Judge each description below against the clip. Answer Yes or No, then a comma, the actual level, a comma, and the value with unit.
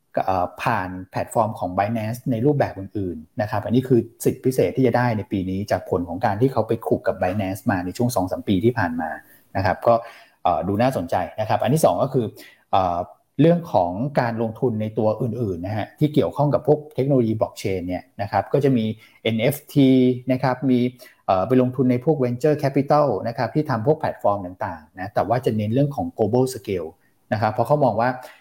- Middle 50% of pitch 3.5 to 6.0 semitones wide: Yes, average, 4.0 semitones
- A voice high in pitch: No, low, 120 Hz